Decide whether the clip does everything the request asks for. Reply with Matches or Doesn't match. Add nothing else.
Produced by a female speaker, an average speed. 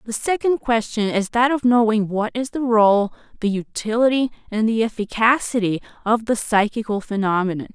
Matches